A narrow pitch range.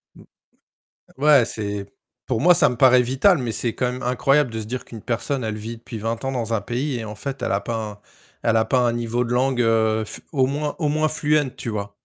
No: average, 3.1 semitones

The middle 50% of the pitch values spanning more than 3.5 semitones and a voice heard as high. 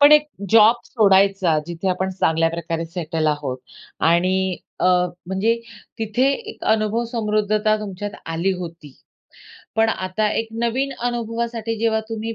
Yes: average, 4.5 semitones; high, 205 Hz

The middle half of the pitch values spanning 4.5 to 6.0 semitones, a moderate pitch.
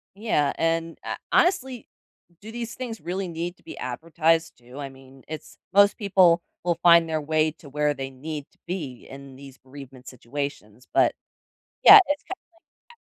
Yes: wide, 5.4 semitones; medium, 160 Hz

